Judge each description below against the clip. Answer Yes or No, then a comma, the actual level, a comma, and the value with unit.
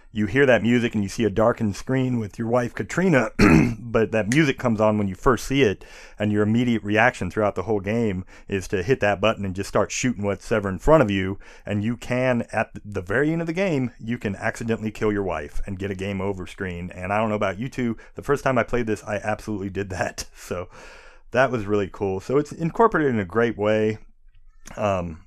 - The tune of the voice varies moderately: Yes, average, 3.2 semitones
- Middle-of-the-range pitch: No, low, 110 Hz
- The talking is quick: Yes, fast, 235 wpm